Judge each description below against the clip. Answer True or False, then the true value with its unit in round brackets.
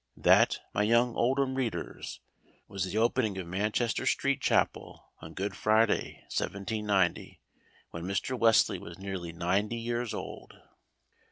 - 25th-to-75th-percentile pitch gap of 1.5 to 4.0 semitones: True (3.6 semitones)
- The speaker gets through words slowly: True (125 wpm)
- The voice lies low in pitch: True (105 Hz)